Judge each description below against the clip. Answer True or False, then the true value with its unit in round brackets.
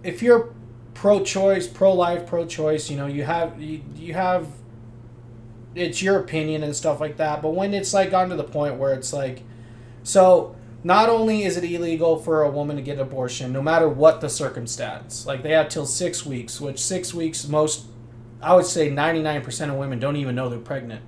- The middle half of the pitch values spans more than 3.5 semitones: True (5.3 semitones)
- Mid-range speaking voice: True (150 Hz)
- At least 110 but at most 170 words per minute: False (205 wpm)